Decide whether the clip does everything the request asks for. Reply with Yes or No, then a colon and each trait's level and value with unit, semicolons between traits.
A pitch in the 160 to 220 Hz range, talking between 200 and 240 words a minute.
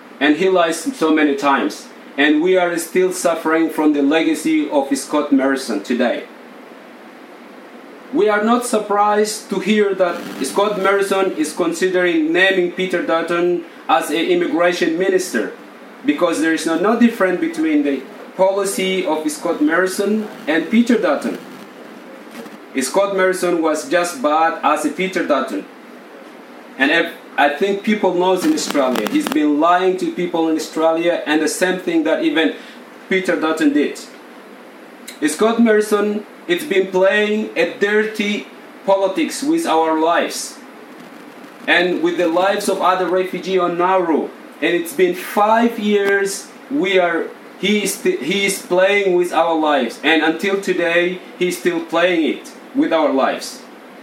No: high, 190 Hz; average, 145 wpm